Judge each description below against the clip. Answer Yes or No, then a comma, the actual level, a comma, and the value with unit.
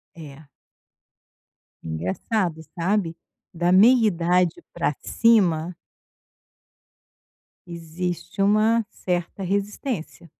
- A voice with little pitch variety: No, average, 3.8 semitones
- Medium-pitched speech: Yes, medium, 180 Hz